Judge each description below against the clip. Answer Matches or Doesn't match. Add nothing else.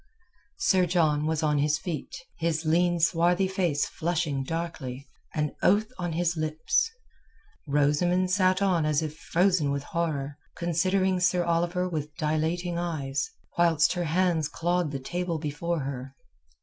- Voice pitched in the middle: Matches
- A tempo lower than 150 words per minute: Matches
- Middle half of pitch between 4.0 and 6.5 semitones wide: Doesn't match